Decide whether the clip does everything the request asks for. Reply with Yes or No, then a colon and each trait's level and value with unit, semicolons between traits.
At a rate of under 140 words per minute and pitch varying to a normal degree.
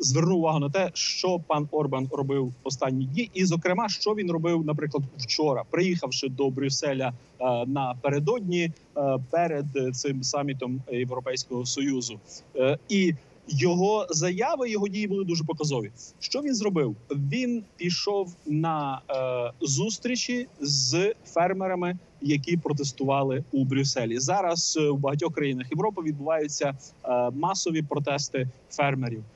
Yes: average, 115 wpm; average, 4.7 semitones